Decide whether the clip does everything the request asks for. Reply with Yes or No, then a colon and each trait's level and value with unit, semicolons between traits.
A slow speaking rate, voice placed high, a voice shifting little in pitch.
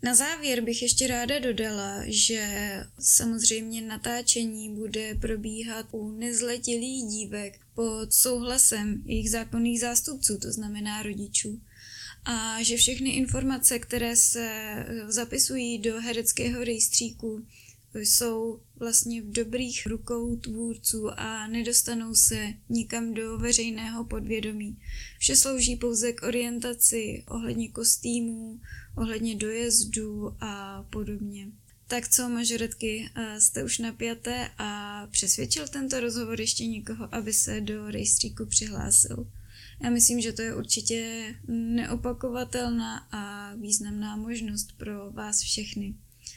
Yes: slow, 110 wpm; high, 225 Hz; narrow, 2.0 semitones